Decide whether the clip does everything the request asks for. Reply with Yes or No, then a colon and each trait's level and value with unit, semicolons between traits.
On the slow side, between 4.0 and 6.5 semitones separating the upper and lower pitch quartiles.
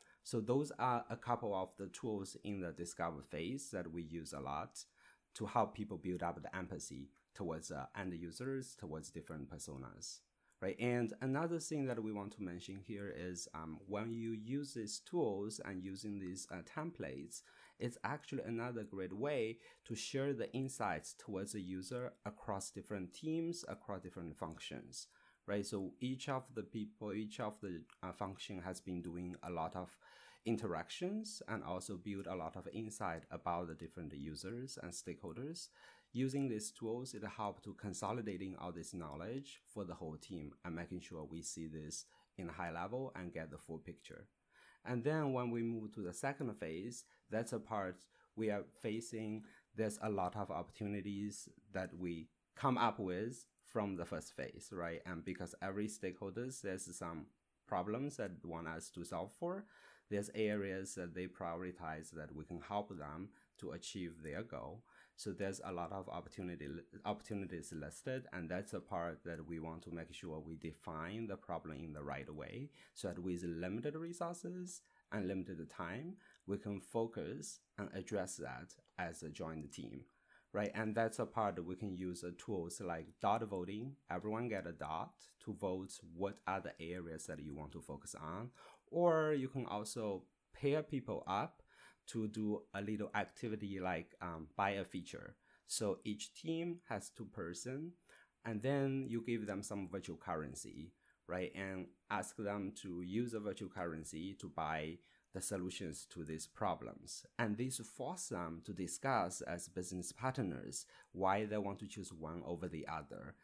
No: average, 170 wpm; average, 4.6 semitones